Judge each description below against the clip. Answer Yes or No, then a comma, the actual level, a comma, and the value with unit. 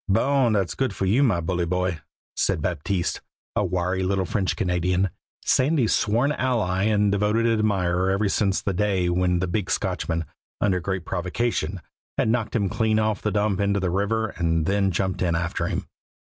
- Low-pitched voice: Yes, very low, 95 Hz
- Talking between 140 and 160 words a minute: No, average, 175 wpm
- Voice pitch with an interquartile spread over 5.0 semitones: No, average, 3.0 semitones